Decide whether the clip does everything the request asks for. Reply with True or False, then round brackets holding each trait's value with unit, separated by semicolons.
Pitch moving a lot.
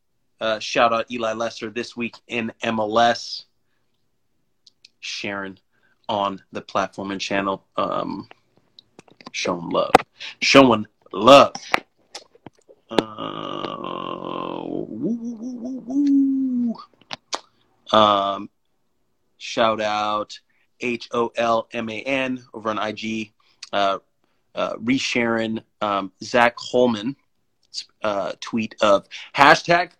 True (6.0 semitones)